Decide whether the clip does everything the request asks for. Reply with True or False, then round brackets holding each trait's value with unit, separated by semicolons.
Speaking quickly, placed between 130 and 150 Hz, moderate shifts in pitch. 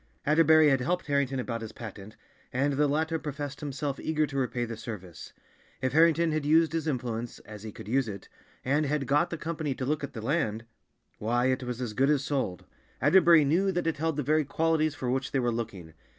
True (210 wpm; 140 Hz; 4.2 semitones)